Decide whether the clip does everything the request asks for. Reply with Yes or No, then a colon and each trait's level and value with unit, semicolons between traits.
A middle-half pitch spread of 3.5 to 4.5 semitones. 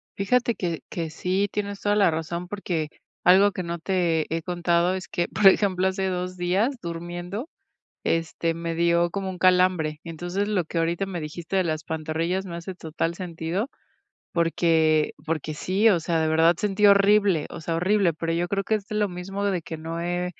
No: average, 2.7 semitones